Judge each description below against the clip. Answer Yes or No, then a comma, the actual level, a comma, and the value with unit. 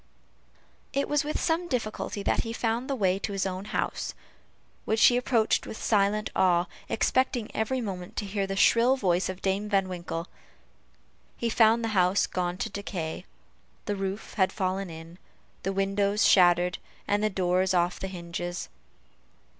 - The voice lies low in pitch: No, high, 195 Hz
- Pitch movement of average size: Yes, average, 3.2 semitones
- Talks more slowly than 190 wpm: Yes, average, 160 wpm